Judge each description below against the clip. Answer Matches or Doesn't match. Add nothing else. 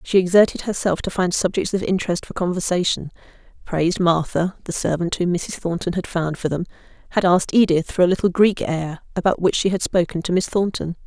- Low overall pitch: Doesn't match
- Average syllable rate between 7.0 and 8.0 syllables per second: Doesn't match